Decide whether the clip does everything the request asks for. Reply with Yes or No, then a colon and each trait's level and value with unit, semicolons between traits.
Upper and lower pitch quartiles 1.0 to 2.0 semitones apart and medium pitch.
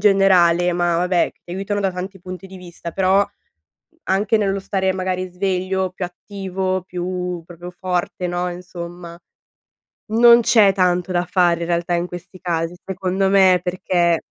Yes: narrow, 1.5 semitones; medium, 180 Hz